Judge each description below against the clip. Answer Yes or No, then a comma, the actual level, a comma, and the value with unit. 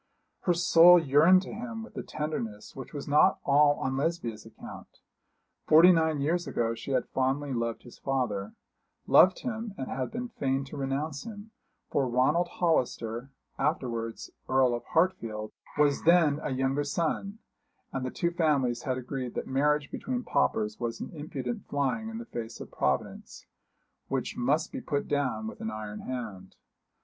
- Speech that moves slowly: No, average, 165 wpm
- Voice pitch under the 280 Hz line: Yes, medium, 140 Hz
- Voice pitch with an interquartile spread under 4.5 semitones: No, average, 5.3 semitones